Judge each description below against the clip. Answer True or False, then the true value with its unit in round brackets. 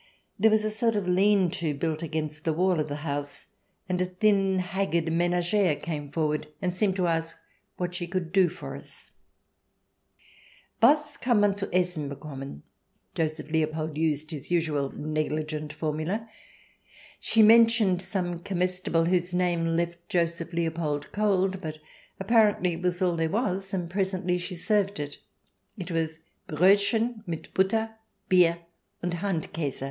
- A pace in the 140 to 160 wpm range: True (150 wpm)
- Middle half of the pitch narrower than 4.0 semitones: True (3.3 semitones)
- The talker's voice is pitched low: False (175 Hz)